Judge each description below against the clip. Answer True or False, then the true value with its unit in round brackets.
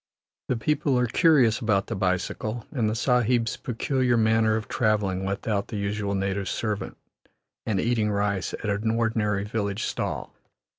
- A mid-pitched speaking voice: False (110 Hz)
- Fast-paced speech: False (150 wpm)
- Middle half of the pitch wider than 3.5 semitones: False (2.5 semitones)